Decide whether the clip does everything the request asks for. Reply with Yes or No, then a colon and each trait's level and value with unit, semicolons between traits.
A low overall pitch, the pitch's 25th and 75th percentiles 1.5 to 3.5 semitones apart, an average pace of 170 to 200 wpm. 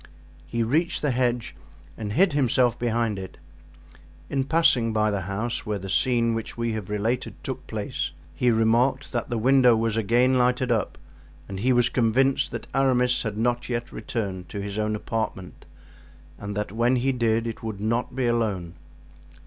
Yes: low, 115 Hz; narrow, 2.6 semitones; average, 175 wpm